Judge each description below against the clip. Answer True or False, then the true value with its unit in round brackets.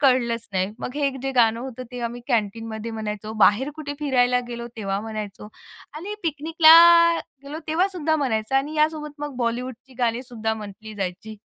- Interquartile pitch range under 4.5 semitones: False (5.0 semitones)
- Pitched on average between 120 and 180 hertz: False (245 Hz)